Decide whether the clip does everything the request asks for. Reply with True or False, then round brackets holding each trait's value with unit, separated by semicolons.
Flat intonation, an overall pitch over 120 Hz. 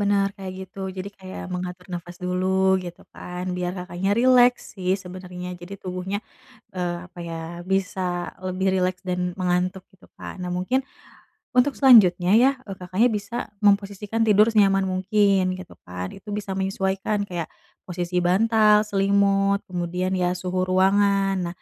True (1.8 semitones; 190 Hz)